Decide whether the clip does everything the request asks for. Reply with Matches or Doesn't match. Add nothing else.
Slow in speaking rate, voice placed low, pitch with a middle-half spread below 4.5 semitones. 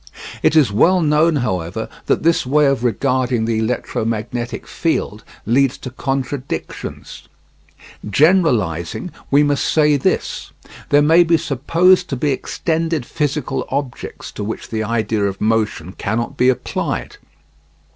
Doesn't match